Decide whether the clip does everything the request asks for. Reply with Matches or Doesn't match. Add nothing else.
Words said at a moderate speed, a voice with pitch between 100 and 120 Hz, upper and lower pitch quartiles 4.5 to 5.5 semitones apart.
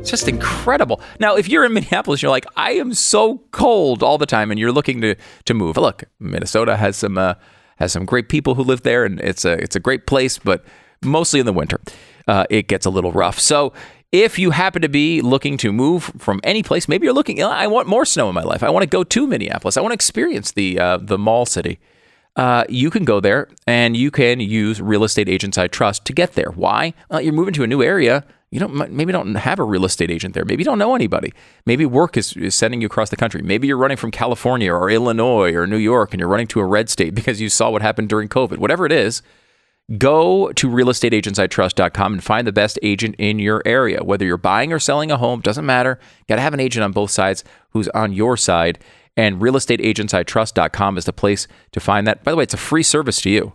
Doesn't match